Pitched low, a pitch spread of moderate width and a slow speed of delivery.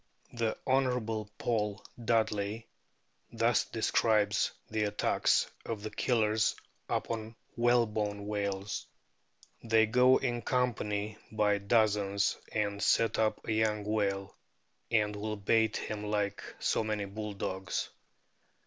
No: low, 110 Hz; narrow, 1.6 semitones; slow, 115 wpm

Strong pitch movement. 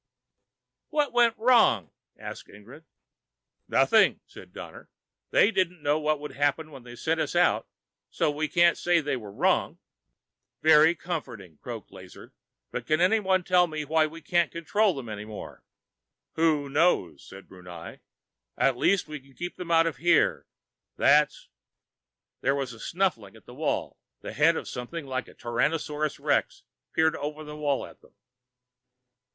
No: average, 4.7 semitones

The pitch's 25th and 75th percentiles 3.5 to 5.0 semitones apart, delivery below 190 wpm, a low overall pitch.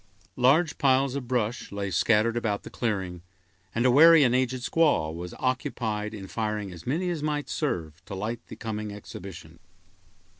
Yes: average, 4.5 semitones; average, 165 wpm; low, 115 Hz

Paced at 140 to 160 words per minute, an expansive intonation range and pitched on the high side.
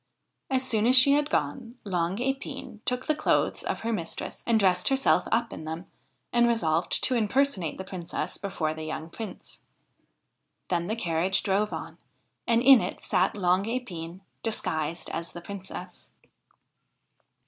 Yes: average, 155 wpm; wide, 5.8 semitones; high, 200 Hz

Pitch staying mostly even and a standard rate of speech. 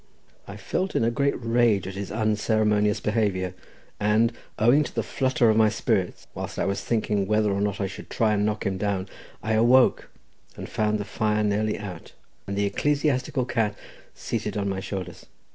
Yes: narrow, 2.3 semitones; average, 185 wpm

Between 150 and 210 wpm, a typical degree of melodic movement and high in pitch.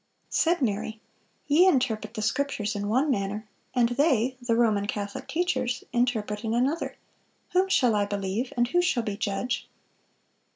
Yes: average, 155 wpm; average, 4.0 semitones; high, 240 Hz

